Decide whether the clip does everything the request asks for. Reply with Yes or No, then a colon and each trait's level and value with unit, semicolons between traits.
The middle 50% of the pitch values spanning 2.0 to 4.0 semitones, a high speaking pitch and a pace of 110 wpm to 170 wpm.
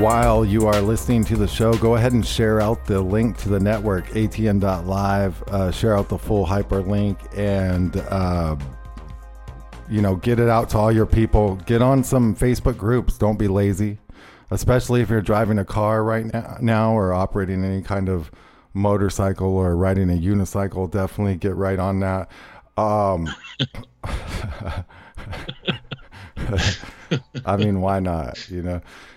No: narrow, 2.6 semitones; low, 100 Hz; average, 150 wpm